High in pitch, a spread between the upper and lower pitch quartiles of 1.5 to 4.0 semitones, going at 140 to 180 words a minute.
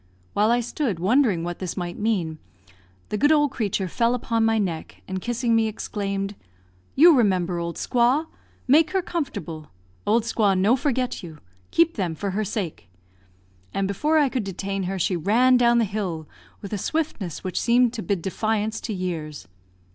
No: high, 210 Hz; average, 4.8 semitones; average, 175 wpm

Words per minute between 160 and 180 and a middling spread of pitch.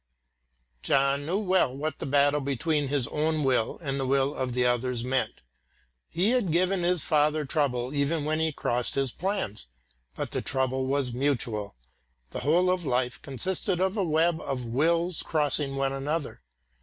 Yes: average, 165 wpm; average, 3.8 semitones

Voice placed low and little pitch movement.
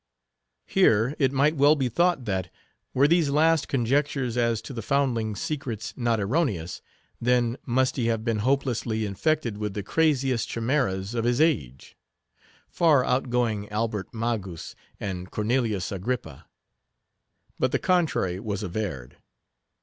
No: low, 120 Hz; average, 4.7 semitones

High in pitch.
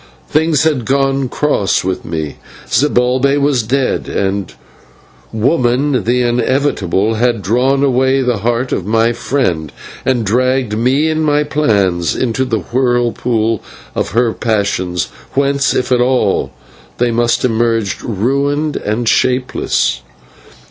No: low, 125 Hz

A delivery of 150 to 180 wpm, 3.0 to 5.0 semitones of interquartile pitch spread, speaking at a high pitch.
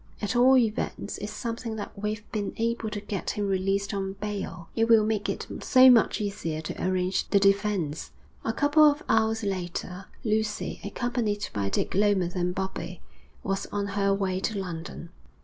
No: average, 170 wpm; narrow, 2.5 semitones; high, 205 Hz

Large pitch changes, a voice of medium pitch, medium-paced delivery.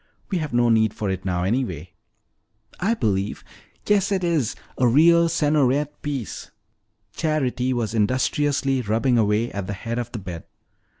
No: wide, 5.8 semitones; low, 125 Hz; average, 155 wpm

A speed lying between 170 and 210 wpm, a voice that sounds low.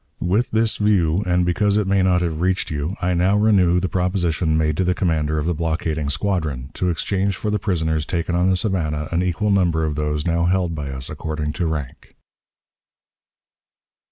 Yes: average, 190 wpm; very low, 85 Hz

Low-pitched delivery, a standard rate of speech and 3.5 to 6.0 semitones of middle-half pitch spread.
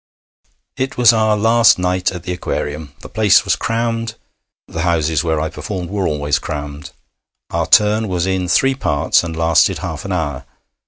Yes: very low, 90 Hz; average, 170 wpm; average, 5.2 semitones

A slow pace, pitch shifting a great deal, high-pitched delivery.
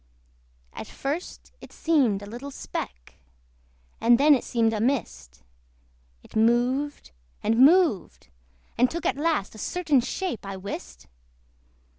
Yes: slow, 130 wpm; wide, 5.7 semitones; high, 245 Hz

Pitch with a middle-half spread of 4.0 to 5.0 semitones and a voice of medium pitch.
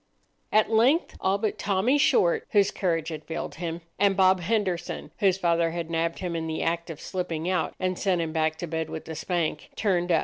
No: average, 2.7 semitones; medium, 175 Hz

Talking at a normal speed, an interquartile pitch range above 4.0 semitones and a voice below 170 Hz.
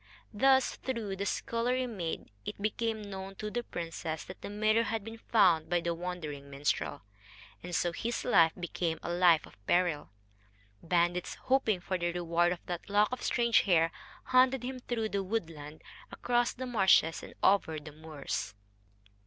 No: average, 170 wpm; average, 5.3 semitones; medium, 185 Hz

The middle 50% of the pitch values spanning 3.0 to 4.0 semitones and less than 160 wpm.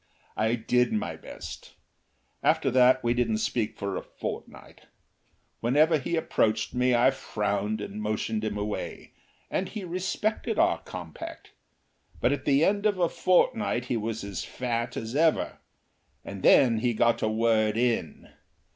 No: average, 4.6 semitones; average, 150 wpm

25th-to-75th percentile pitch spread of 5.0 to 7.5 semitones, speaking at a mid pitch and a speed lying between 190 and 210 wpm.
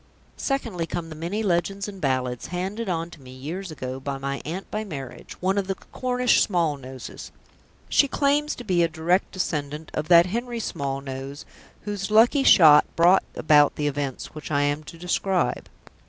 No: wide, 5.4 semitones; medium, 170 Hz; average, 170 wpm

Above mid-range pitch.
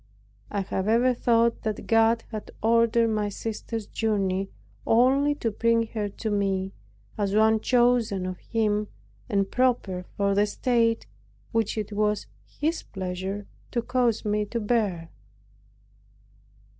Yes: high, 220 Hz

